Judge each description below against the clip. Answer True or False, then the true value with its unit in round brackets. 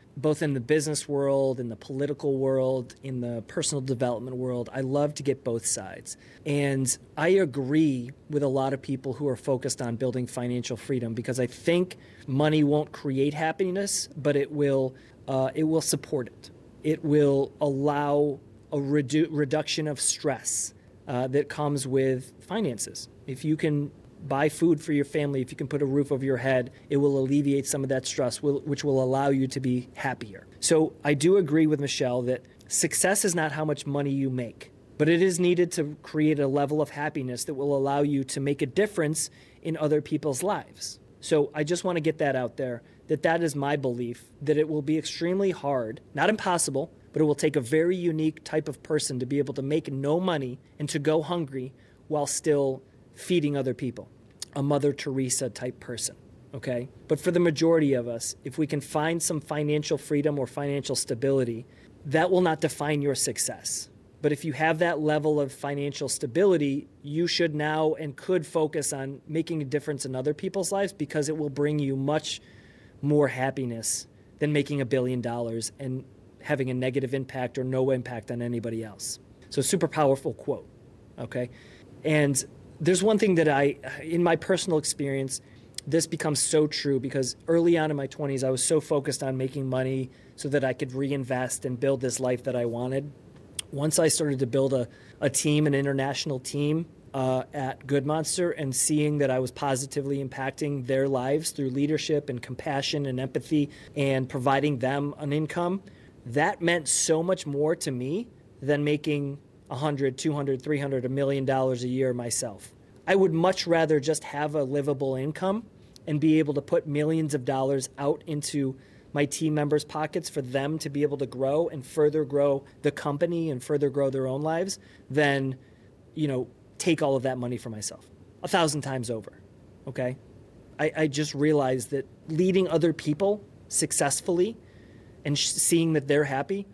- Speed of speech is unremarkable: True (185 wpm)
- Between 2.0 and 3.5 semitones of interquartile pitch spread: True (2.9 semitones)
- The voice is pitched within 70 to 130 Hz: False (140 Hz)